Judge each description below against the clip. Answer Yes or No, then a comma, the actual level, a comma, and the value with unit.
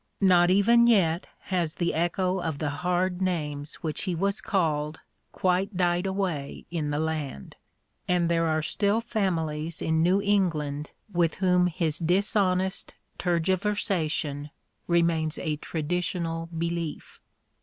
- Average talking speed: No, slow, 125 wpm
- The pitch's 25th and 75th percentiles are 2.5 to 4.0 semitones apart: Yes, average, 2.9 semitones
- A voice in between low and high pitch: Yes, medium, 170 Hz